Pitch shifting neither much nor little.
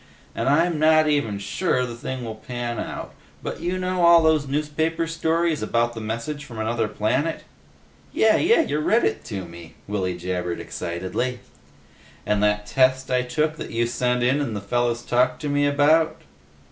No: wide, 6.0 semitones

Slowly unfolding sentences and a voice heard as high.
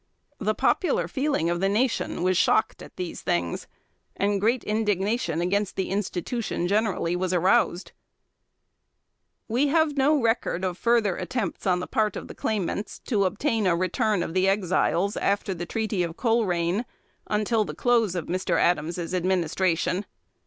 No: average, 150 wpm; high, 195 Hz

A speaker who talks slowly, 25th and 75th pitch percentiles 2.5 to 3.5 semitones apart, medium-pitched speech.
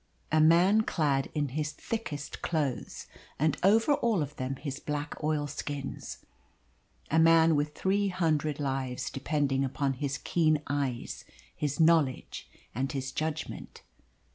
Yes: slow, 130 wpm; average, 2.9 semitones; medium, 150 Hz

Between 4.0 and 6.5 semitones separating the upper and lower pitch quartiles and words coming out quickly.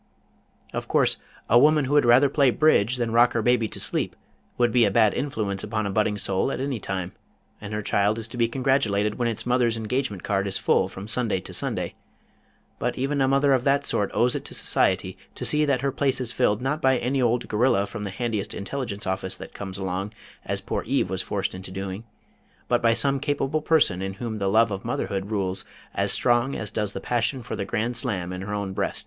Yes: average, 4.4 semitones; fast, 225 wpm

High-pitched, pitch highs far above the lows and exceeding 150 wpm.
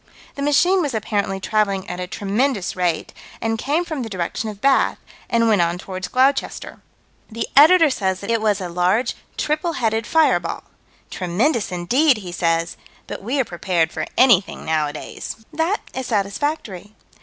Yes: high, 215 Hz; wide, 6.7 semitones; average, 160 wpm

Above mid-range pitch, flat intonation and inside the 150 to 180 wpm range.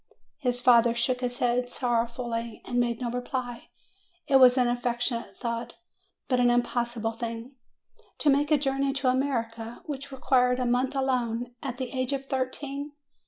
Yes: high, 245 Hz; narrow, 1.9 semitones; average, 165 wpm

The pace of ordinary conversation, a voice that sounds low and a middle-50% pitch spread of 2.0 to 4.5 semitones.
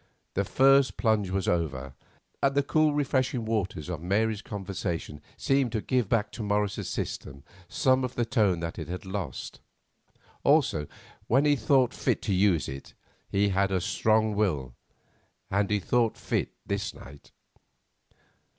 No: average, 150 wpm; low, 105 Hz; average, 5.1 semitones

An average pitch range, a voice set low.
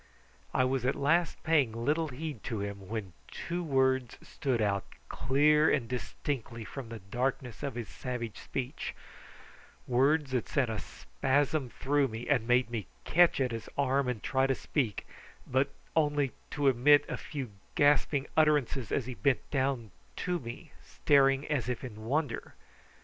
Yes: average, 3.6 semitones; low, 130 Hz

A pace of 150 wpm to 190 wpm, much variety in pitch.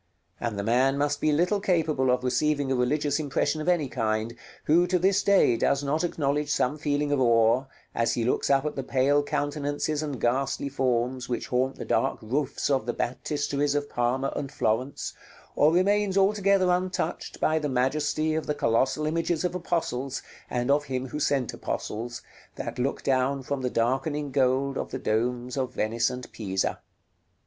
No: average, 180 wpm; average, 3.3 semitones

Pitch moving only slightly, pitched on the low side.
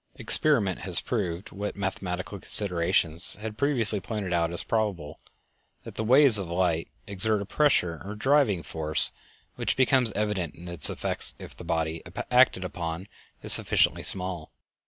No: average, 4.2 semitones; very low, 95 Hz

